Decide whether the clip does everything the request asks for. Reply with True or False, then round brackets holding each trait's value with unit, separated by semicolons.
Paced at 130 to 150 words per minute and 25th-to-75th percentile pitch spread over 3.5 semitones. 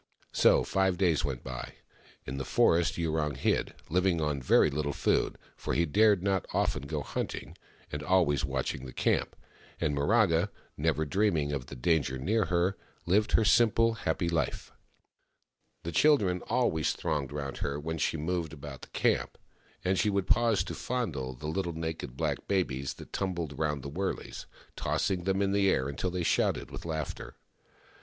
False (175 wpm; 4.9 semitones)